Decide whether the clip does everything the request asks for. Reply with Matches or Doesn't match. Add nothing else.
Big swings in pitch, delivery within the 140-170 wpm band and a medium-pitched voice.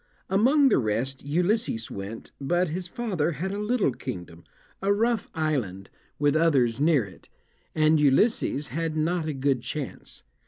Matches